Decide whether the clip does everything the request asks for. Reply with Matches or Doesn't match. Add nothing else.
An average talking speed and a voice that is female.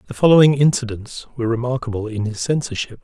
Doesn't match